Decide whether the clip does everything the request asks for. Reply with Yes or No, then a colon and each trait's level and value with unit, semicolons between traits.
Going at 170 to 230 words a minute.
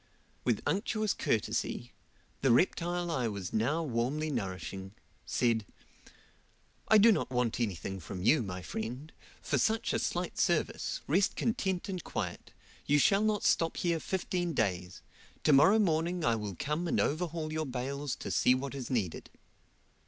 No: average, 150 wpm